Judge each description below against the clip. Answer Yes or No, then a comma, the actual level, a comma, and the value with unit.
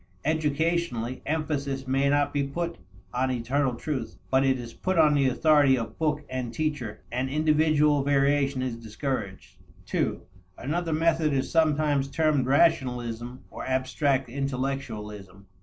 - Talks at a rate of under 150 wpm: Yes, slow, 135 wpm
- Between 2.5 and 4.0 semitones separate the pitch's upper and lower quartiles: Yes, average, 3.1 semitones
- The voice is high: No, medium, 140 Hz